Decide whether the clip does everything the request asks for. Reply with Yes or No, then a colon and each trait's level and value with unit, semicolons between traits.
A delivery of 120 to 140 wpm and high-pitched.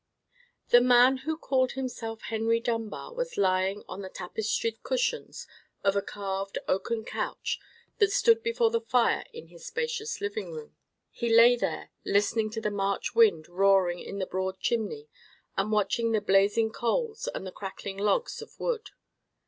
No: average, 160 wpm; high, 225 Hz